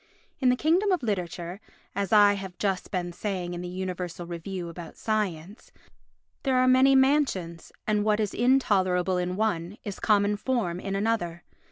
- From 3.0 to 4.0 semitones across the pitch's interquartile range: Yes, average, 3.7 semitones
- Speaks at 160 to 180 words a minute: Yes, average, 165 wpm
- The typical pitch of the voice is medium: No, high, 195 Hz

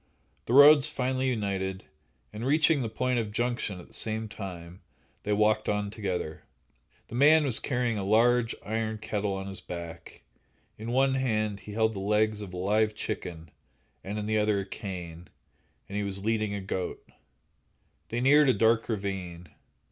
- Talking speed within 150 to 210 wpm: Yes, average, 170 wpm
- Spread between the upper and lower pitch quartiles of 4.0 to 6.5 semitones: No, average, 3.5 semitones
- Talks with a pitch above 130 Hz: No, low, 105 Hz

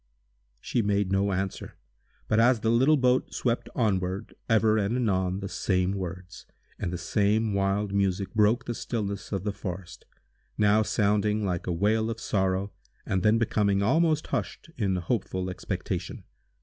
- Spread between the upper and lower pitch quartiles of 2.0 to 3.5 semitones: Yes, average, 2.7 semitones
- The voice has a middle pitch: No, low, 100 Hz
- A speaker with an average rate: Yes, average, 155 wpm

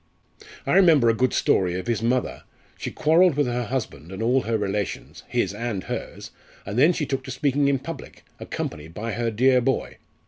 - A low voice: Yes, low, 120 Hz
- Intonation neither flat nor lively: Yes, average, 4.4 semitones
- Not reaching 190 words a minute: No, average, 195 wpm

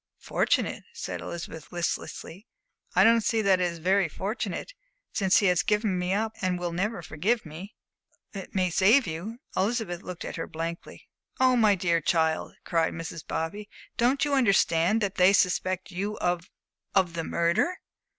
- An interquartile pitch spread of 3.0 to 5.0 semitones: Yes, average, 3.9 semitones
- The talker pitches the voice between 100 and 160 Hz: No, medium, 185 Hz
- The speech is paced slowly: No, average, 170 wpm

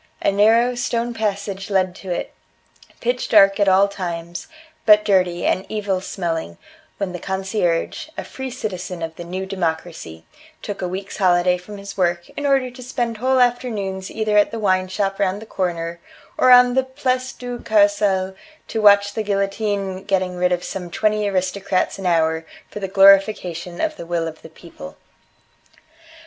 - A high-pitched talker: Yes, high, 195 Hz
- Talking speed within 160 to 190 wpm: Yes, average, 170 wpm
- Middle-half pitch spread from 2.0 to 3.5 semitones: Yes, average, 3.1 semitones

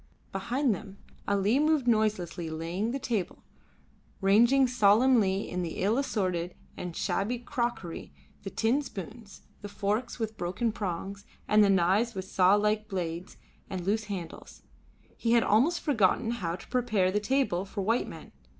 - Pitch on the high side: Yes, high, 210 Hz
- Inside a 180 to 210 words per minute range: No, average, 150 wpm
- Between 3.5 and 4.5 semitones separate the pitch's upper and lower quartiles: Yes, average, 3.9 semitones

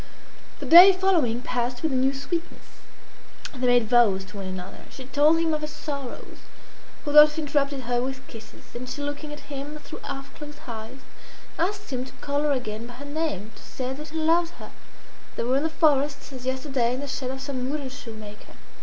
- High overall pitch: Yes, very high, 275 Hz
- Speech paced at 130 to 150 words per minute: No, average, 200 wpm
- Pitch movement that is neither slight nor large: Yes, average, 3.4 semitones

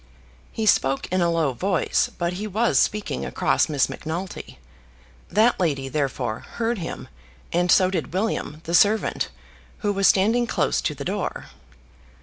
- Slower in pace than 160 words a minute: Yes, average, 150 wpm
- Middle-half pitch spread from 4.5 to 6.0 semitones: Yes, average, 5.2 semitones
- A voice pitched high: No, medium, 180 Hz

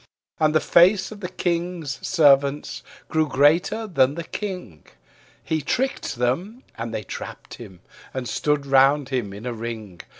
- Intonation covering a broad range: Yes, wide, 6.1 semitones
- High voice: No, medium, 145 Hz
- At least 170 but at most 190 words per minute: No, average, 155 wpm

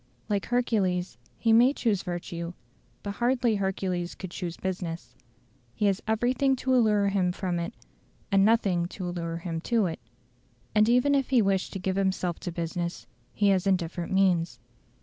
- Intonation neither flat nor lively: Yes, average, 4.0 semitones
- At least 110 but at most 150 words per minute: No, average, 165 wpm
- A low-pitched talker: No, high, 190 Hz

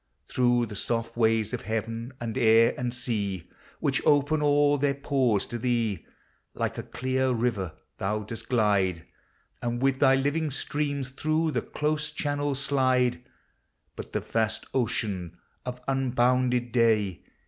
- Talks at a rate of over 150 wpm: No, average, 140 wpm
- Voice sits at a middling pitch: No, low, 125 Hz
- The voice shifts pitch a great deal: No, average, 3.4 semitones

